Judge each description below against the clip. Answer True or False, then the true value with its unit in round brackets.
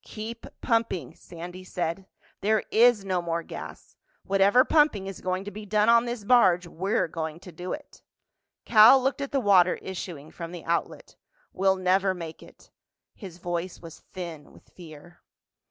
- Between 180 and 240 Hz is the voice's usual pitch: True (185 Hz)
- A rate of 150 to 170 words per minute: True (160 wpm)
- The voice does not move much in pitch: False (3.8 semitones)